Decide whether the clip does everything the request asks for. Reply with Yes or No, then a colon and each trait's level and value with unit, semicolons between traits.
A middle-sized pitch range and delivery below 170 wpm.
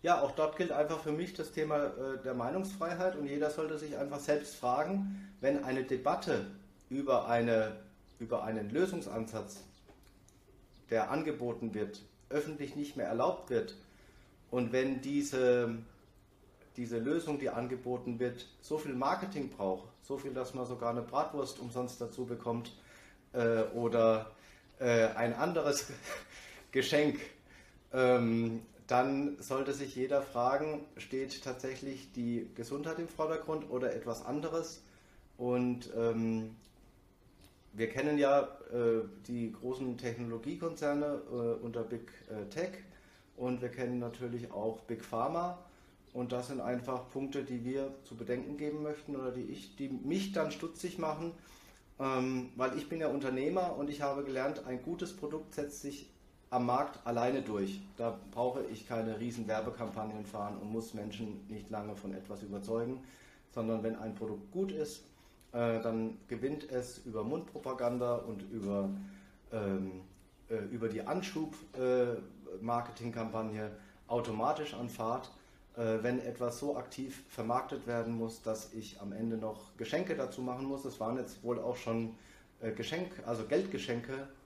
Yes: average, 4.0 semitones; average, 145 wpm